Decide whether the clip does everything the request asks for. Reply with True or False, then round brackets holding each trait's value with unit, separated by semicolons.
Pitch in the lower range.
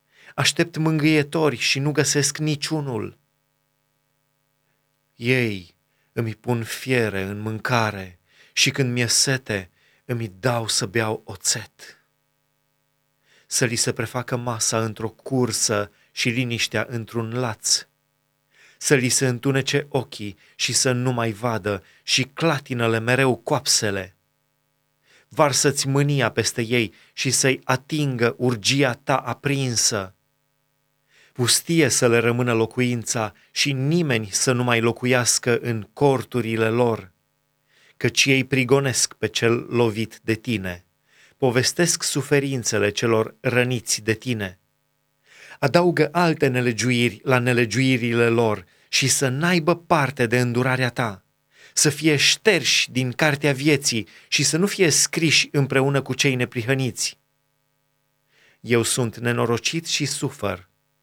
True (125 Hz)